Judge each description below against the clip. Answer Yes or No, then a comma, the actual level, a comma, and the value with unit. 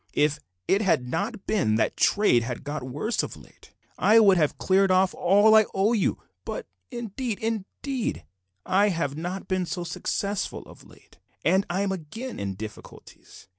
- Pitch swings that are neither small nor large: No, wide, 5.7 semitones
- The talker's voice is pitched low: No, high, 190 Hz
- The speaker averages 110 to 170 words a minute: Yes, average, 165 wpm